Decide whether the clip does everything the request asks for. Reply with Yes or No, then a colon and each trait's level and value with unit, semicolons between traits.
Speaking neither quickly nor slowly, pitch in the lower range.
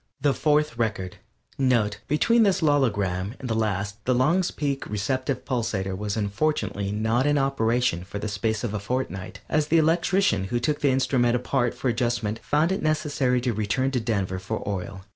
Yes: average, 180 wpm; low, 120 Hz